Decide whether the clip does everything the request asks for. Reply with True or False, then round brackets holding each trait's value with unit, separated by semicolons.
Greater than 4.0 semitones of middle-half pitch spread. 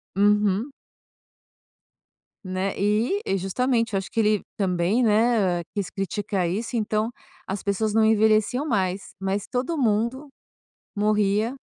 False (2.7 semitones)